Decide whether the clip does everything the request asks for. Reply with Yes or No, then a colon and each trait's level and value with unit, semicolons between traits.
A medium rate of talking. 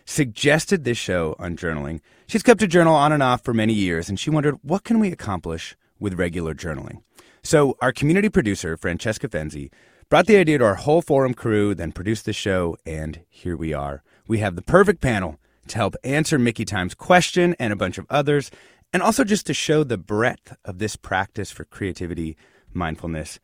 Yes: average, 195 wpm